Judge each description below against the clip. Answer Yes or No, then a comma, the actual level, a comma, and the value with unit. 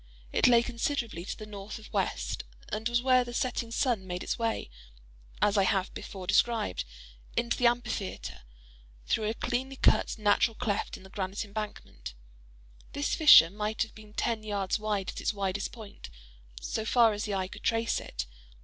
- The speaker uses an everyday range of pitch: Yes, average, 3.1 semitones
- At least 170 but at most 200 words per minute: Yes, average, 175 wpm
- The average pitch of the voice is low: No, high, 215 Hz